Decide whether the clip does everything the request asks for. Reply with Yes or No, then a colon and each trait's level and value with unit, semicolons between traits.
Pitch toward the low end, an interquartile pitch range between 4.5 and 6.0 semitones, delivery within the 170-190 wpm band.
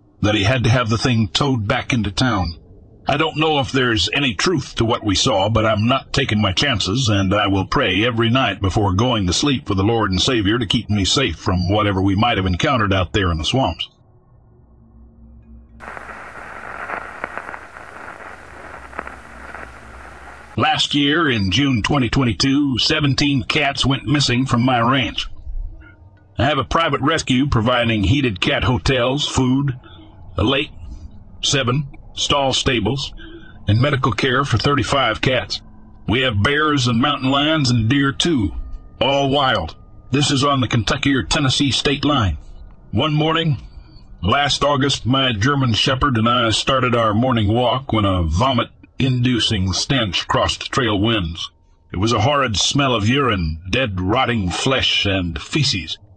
No: low, 120 Hz; average, 5.1 semitones; average, 155 wpm